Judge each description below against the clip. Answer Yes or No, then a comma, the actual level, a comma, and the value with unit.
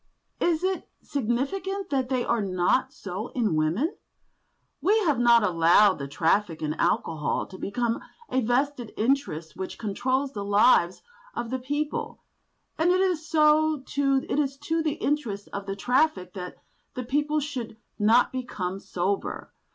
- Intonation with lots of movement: Yes, wide, 6.6 semitones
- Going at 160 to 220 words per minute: No, slow, 135 wpm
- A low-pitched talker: No, high, 245 Hz